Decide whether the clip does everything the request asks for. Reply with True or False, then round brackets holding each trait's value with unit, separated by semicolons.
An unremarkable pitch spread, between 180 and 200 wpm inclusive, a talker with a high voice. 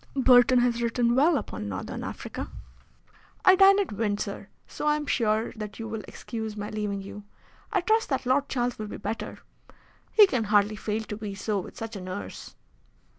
True (4.1 semitones; 185 wpm; 225 Hz)